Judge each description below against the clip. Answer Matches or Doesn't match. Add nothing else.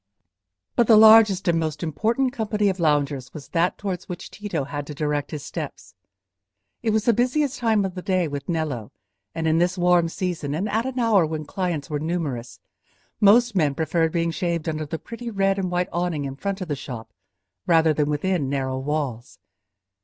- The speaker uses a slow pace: Doesn't match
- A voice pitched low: Doesn't match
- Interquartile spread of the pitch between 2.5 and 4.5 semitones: Doesn't match